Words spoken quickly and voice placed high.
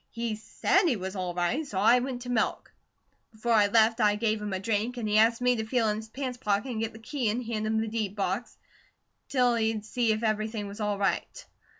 Yes: fast, 235 wpm; high, 220 Hz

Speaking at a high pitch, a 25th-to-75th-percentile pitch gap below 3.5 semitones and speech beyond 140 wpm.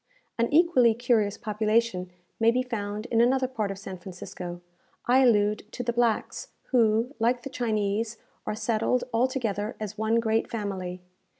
Yes: high, 225 Hz; average, 2.7 semitones; average, 155 wpm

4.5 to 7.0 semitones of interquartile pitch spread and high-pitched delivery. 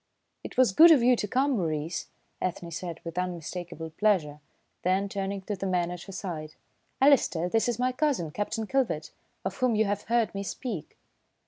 Yes: wide, 5.4 semitones; high, 195 Hz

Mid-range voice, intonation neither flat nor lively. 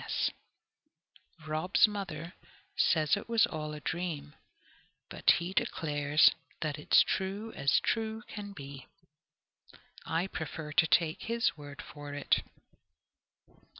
Yes: medium, 160 Hz; average, 4.8 semitones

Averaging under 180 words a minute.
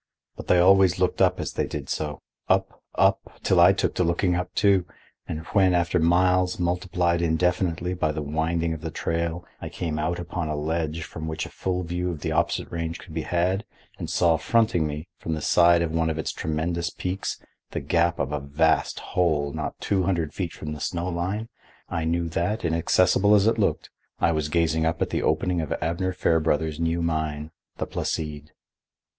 No: average, 195 wpm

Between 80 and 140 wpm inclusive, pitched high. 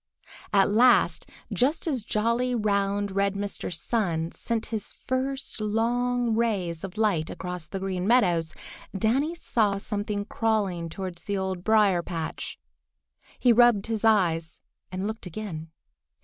Yes: slow, 135 wpm; high, 205 Hz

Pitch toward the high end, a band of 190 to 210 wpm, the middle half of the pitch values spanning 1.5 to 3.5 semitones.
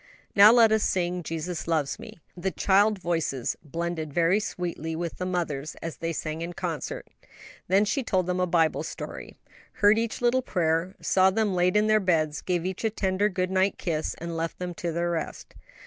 No: medium, 180 Hz; average, 195 wpm; average, 2.8 semitones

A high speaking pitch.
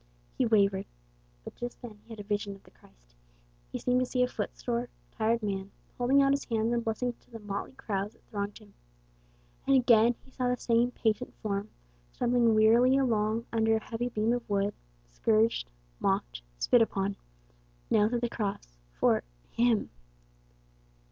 Yes: high, 225 Hz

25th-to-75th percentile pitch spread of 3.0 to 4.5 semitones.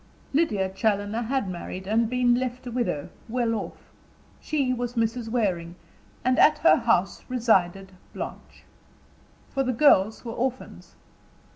Yes: average, 3.9 semitones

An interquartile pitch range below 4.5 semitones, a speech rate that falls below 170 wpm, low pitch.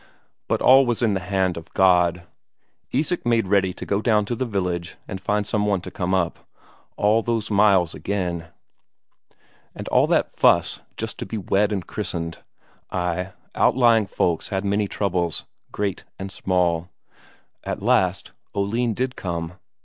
Yes: average, 3.0 semitones; average, 155 wpm; low, 100 Hz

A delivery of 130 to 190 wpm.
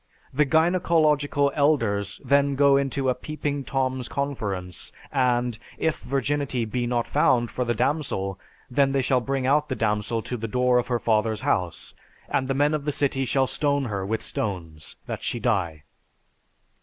Yes: average, 170 wpm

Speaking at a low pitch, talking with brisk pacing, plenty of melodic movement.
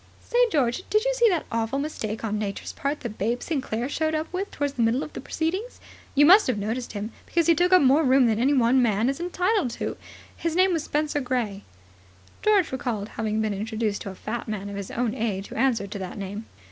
No: very high, 250 Hz; fast, 230 wpm; wide, 6.5 semitones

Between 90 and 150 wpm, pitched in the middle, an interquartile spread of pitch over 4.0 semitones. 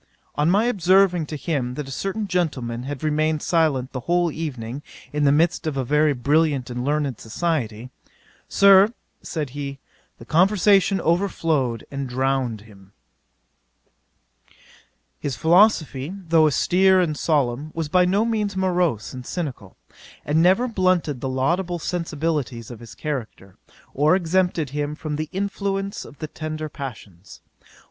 Yes: average, 140 wpm; medium, 155 Hz; average, 5.2 semitones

